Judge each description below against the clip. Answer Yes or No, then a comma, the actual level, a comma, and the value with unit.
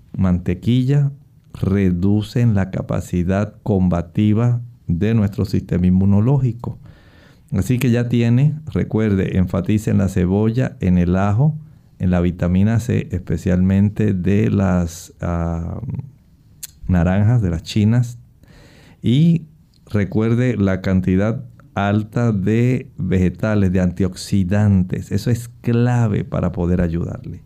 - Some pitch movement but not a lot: Yes, average, 4.6 semitones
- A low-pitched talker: Yes, low, 100 Hz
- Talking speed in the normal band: No, slow, 105 wpm